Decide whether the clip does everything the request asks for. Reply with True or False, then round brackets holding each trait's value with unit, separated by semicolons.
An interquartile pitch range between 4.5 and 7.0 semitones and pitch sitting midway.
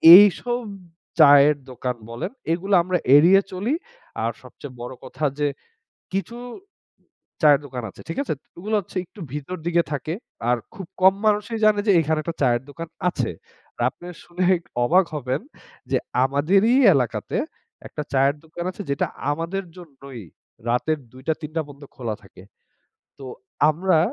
True (5.2 semitones; 160 Hz)